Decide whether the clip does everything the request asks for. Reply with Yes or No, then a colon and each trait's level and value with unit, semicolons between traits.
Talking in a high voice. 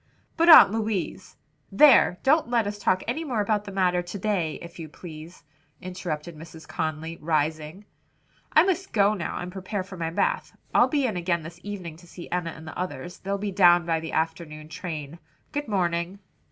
No: medium, 180 Hz